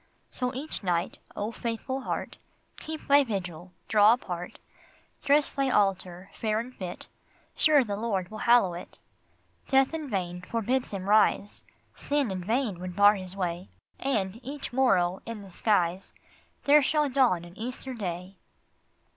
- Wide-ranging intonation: Yes, wide, 6.0 semitones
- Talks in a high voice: Yes, high, 210 Hz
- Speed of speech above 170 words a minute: No, average, 150 wpm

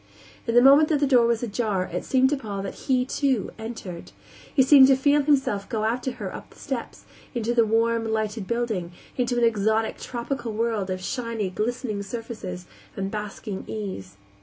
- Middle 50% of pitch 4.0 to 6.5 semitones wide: No, average, 3.3 semitones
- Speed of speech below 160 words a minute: No, average, 185 wpm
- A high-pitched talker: Yes, high, 230 Hz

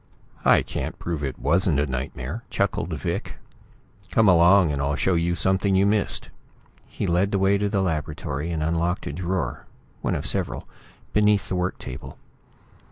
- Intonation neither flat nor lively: Yes, average, 4.1 semitones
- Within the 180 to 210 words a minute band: No, average, 165 wpm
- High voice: No, very low, 85 Hz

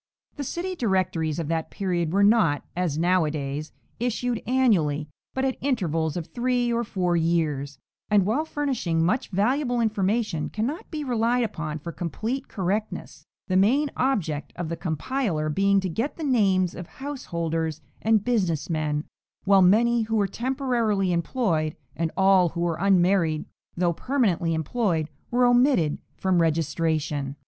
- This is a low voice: No, high, 190 Hz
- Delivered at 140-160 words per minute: Yes, average, 155 wpm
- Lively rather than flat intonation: Yes, wide, 6.6 semitones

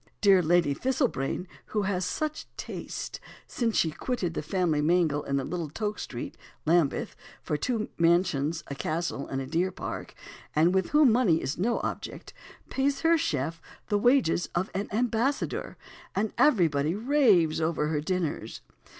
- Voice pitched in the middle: Yes, medium, 180 Hz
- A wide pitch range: Yes, wide, 6.1 semitones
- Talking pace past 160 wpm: No, average, 150 wpm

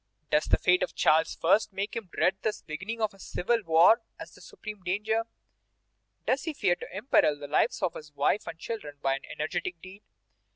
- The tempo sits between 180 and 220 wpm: Yes, average, 195 wpm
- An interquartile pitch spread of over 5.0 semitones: Yes, wide, 5.5 semitones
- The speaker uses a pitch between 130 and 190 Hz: Yes, medium, 185 Hz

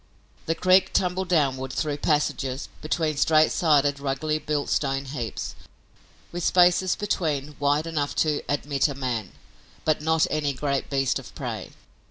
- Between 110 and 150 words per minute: Yes, average, 145 wpm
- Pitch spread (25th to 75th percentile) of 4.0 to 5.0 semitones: No, average, 2.7 semitones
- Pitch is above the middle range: No, medium, 150 Hz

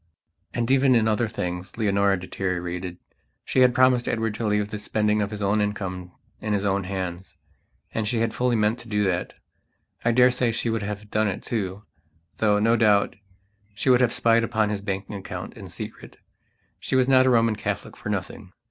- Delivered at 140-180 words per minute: No, average, 190 wpm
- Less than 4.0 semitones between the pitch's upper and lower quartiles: Yes, average, 2.8 semitones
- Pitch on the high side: No, low, 105 Hz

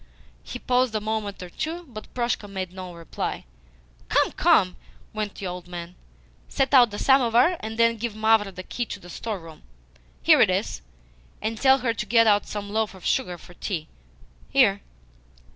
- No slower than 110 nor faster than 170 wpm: No, average, 180 wpm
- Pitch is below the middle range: No, high, 215 Hz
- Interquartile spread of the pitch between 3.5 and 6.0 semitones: Yes, average, 4.2 semitones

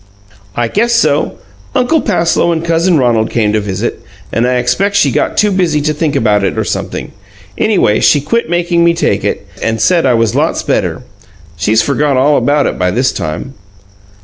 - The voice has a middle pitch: Yes, medium, 145 Hz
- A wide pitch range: Yes, wide, 7.0 semitones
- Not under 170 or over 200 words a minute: Yes, average, 190 wpm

